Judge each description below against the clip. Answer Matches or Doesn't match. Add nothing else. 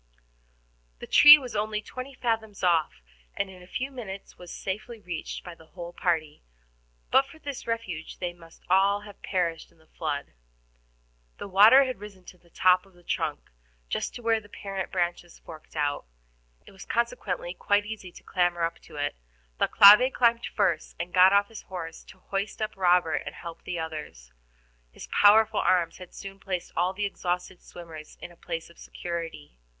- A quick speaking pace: Doesn't match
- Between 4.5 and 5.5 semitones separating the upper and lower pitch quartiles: Doesn't match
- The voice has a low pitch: Doesn't match